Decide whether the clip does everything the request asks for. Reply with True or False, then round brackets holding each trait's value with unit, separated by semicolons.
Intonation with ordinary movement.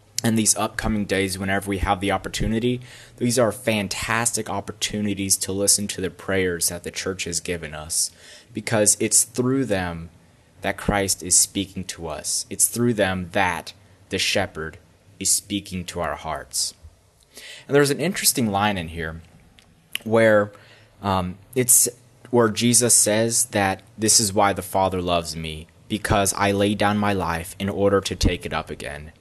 True (3.1 semitones)